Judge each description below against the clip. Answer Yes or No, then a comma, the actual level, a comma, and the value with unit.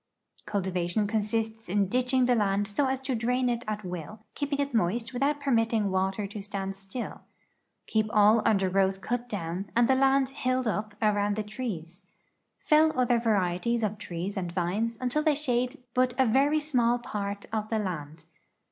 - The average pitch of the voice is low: No, high, 220 Hz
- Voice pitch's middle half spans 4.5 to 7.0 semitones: No, average, 4.1 semitones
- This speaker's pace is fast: No, average, 165 wpm